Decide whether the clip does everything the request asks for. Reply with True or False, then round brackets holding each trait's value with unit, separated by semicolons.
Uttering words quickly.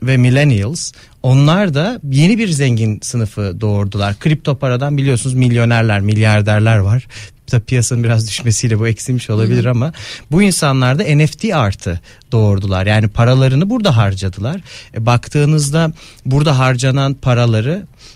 False (125 wpm)